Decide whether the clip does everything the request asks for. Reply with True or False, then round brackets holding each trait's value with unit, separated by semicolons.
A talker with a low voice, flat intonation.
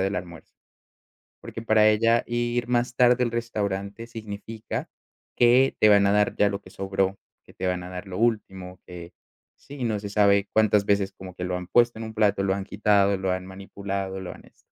False (100 Hz; 3.0 semitones)